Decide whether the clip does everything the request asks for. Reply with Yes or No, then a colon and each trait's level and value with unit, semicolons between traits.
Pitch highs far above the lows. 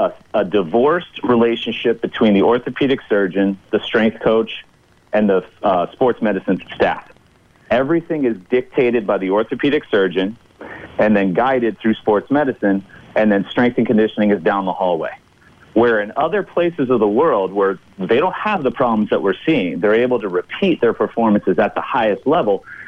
No: average, 4.1 semitones